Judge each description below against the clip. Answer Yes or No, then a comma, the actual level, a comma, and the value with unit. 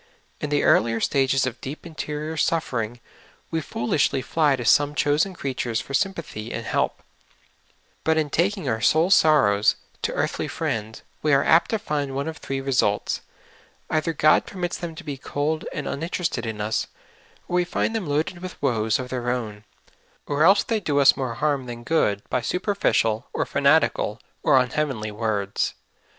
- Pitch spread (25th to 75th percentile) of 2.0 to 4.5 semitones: No, average, 5.0 semitones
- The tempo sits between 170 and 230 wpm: Yes, average, 175 wpm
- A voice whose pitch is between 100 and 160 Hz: Yes, medium, 140 Hz